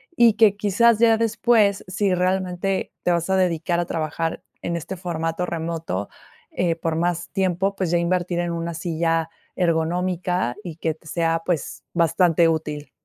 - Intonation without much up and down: Yes, narrow, 2.3 semitones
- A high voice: No, medium, 175 Hz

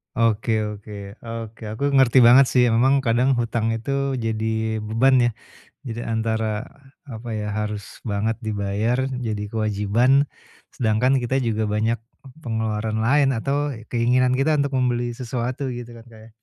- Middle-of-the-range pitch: No, low, 115 Hz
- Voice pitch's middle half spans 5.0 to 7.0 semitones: No, average, 2.7 semitones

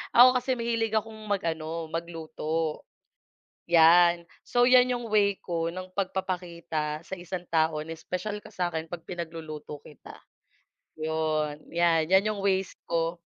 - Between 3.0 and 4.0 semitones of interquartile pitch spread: Yes, average, 3.3 semitones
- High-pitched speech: No, medium, 170 Hz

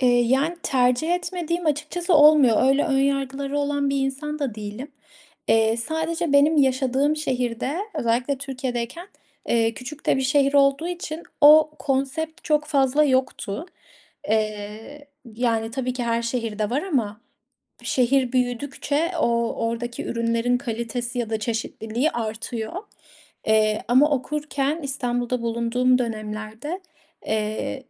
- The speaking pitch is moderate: No, very high, 260 Hz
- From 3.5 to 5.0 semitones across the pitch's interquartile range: Yes, average, 3.9 semitones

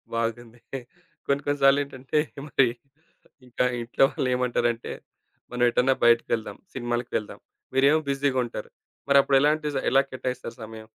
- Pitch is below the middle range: Yes, low, 125 Hz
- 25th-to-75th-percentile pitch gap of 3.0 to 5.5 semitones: No, narrow, 2.5 semitones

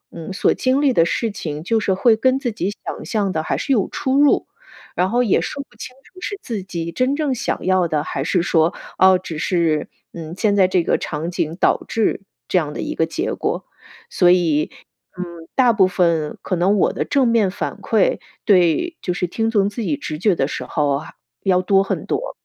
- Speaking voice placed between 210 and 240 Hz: No, medium, 185 Hz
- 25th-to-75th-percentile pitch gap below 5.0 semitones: No, wide, 5.5 semitones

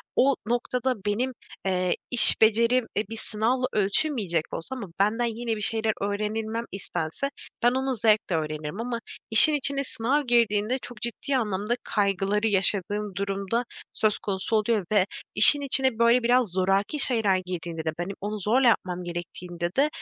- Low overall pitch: No, high, 215 Hz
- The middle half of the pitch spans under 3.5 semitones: No, average, 3.8 semitones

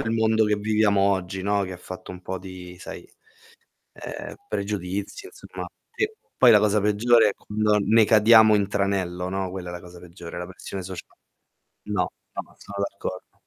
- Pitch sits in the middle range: No, low, 100 Hz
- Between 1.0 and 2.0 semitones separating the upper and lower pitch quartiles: No, narrow, 2.6 semitones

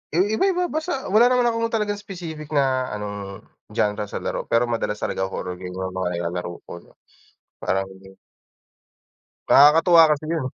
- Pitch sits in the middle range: Yes, medium, 145 Hz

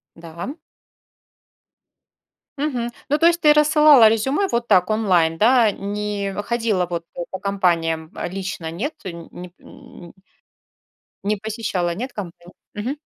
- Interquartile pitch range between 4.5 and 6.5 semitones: Yes, average, 5.3 semitones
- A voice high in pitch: Yes, high, 205 Hz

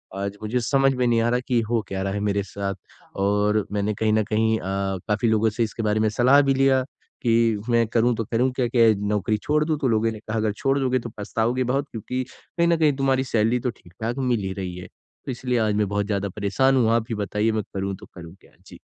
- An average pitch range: Yes, average, 3.2 semitones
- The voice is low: Yes, low, 115 Hz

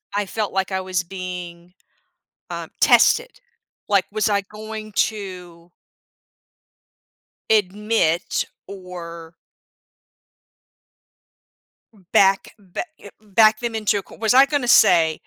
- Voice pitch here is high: Yes, high, 195 Hz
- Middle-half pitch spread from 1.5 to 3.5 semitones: Yes, average, 3.2 semitones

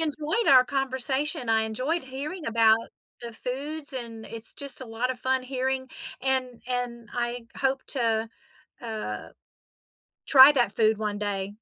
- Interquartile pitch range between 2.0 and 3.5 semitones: Yes, average, 2.9 semitones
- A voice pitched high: Yes, very high, 250 Hz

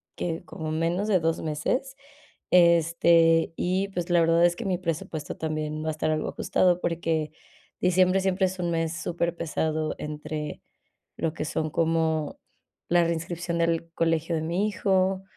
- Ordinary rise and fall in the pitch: No, narrow, 2.0 semitones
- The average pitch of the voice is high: No, medium, 165 Hz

